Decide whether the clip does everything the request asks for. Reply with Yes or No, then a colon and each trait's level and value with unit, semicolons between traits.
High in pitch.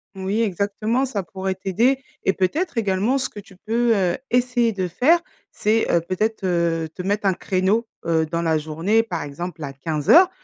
Yes: high, 195 Hz